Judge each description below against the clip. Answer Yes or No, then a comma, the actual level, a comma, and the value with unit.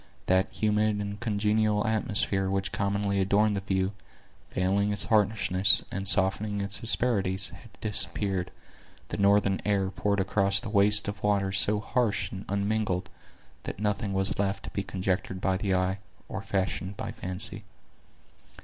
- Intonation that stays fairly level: Yes, narrow, 1.4 semitones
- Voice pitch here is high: No, low, 100 Hz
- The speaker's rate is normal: Yes, average, 150 wpm